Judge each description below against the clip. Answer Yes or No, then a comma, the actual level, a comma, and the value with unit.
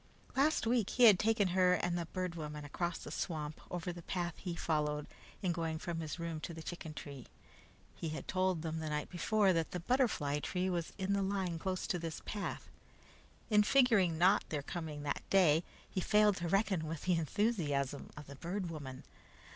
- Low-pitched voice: No, medium, 175 Hz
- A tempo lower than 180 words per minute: No, average, 200 wpm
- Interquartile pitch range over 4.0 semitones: No, average, 3.3 semitones